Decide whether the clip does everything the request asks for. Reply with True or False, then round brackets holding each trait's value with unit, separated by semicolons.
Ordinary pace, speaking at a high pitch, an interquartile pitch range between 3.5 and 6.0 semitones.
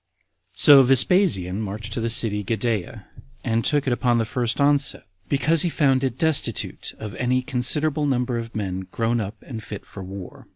False (180 wpm; 120 Hz; 4.2 semitones)